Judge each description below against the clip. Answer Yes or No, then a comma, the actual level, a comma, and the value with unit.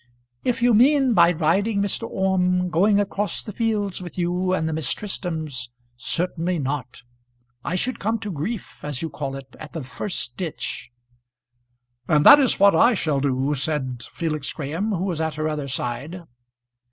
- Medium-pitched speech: Yes, medium, 170 Hz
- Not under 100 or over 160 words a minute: No, average, 175 wpm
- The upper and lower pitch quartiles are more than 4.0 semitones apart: Yes, average, 5.2 semitones